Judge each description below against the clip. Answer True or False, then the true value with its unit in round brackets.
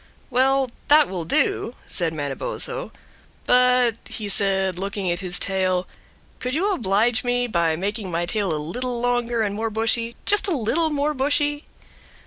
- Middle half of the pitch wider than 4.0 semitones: True (5.0 semitones)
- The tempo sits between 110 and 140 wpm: False (155 wpm)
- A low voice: False (225 Hz)